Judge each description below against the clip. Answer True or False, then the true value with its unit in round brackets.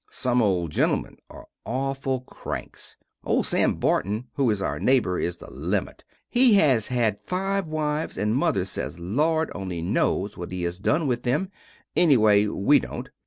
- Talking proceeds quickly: False (165 wpm)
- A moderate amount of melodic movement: False (7.5 semitones)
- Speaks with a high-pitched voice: False (120 Hz)